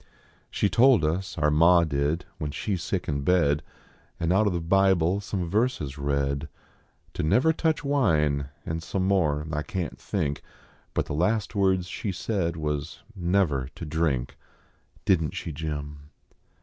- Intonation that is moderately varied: Yes, average, 4.6 semitones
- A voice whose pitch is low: Yes, very low, 85 Hz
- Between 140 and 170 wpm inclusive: Yes, average, 160 wpm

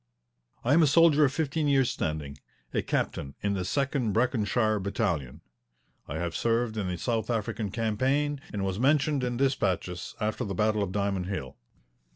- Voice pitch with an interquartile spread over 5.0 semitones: Yes, wide, 5.6 semitones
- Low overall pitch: Yes, low, 110 Hz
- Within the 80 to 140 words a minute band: No, average, 170 wpm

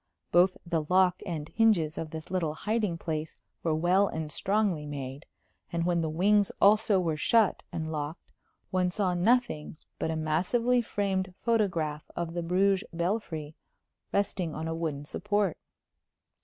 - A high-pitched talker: No, medium, 175 Hz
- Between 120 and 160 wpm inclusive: Yes, average, 150 wpm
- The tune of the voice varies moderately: Yes, average, 4.0 semitones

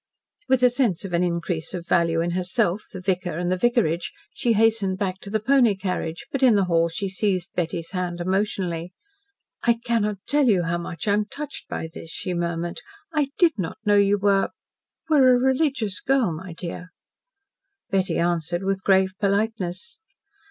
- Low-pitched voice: No, high, 190 Hz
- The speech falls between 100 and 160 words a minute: No, average, 180 wpm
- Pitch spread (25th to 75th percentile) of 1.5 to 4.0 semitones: No, average, 4.4 semitones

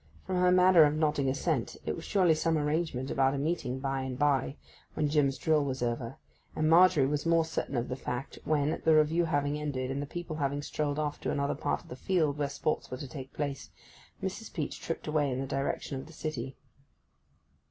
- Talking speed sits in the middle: No, fast, 215 wpm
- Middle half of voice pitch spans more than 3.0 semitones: No, average, 2.7 semitones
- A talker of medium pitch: Yes, medium, 145 Hz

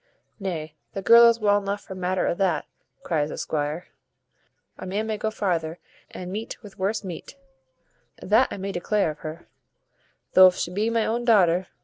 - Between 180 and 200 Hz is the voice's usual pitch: Yes, high, 190 Hz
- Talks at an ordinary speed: Yes, average, 170 wpm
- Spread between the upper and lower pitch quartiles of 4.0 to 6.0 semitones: No, average, 3.5 semitones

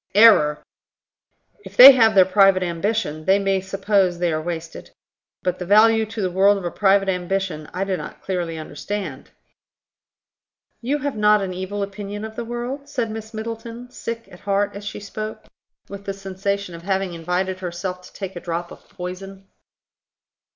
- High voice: Yes, high, 195 Hz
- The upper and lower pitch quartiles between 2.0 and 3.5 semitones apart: Yes, average, 2.9 semitones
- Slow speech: No, average, 170 wpm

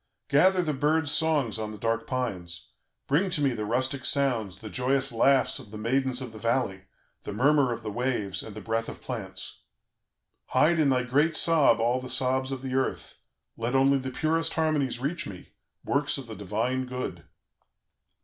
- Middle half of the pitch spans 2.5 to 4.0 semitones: Yes, average, 3.6 semitones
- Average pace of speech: Yes, average, 185 wpm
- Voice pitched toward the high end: No, low, 130 Hz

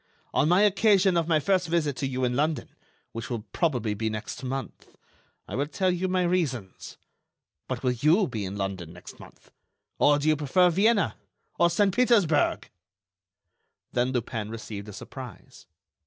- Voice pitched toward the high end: No, medium, 145 Hz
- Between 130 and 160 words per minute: Yes, average, 155 wpm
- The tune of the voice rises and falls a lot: Yes, wide, 7.6 semitones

